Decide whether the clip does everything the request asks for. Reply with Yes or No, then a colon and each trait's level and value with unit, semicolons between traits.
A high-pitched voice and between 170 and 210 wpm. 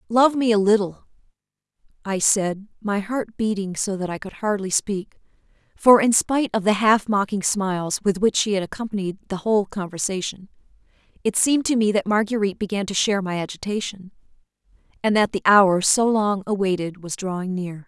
Yes: high, 200 Hz; average, 175 wpm